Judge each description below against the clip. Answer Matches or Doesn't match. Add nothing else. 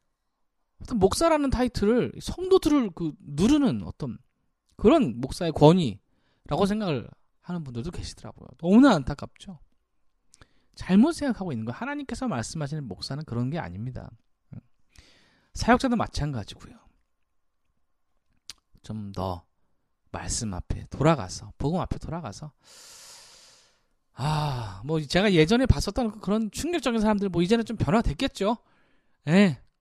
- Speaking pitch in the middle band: Matches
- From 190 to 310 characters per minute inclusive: Matches